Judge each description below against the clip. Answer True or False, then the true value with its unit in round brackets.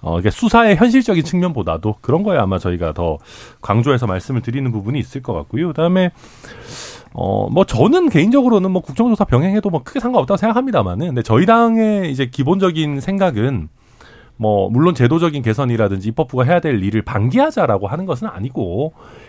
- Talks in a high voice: False (140 Hz)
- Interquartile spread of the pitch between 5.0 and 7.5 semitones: False (8.9 semitones)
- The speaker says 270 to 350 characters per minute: False (410 characters per minute)